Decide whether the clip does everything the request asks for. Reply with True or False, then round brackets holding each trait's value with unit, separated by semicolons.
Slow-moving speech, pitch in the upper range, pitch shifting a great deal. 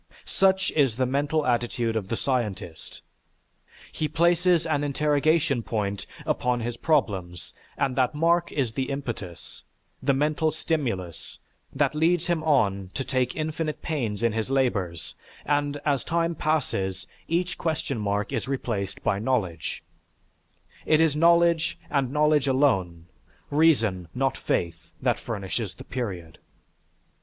False (130 wpm; 135 Hz; 6.7 semitones)